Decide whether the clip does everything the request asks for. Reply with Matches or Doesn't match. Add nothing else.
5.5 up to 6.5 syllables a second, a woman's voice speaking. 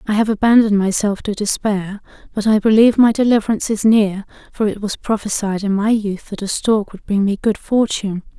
Matches